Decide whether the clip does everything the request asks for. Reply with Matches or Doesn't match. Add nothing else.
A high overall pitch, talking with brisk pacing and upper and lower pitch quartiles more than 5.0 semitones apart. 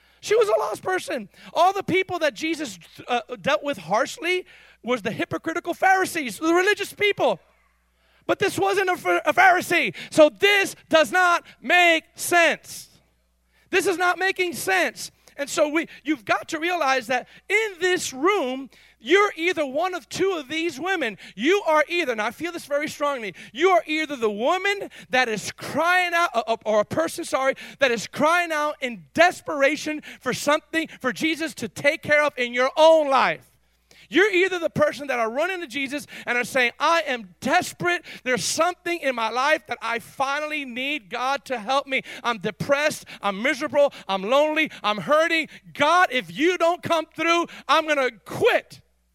Doesn't match